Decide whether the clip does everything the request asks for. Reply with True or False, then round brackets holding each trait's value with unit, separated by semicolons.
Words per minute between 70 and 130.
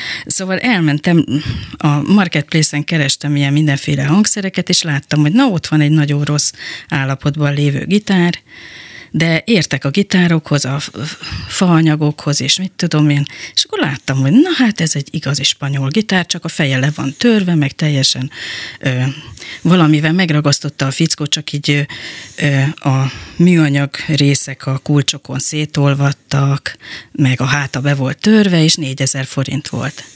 False (145 wpm)